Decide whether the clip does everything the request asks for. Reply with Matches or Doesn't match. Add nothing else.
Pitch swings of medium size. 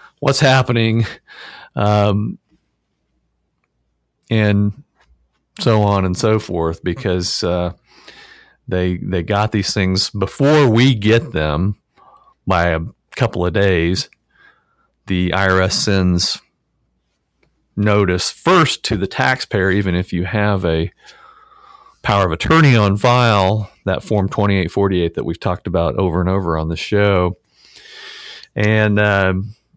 Matches